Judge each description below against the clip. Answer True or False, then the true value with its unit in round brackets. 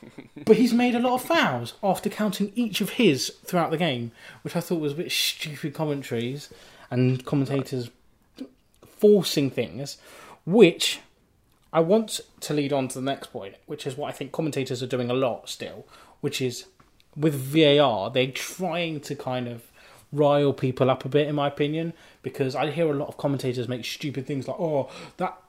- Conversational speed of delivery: True (185 wpm)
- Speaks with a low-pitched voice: False (145 Hz)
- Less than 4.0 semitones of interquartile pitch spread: False (4.4 semitones)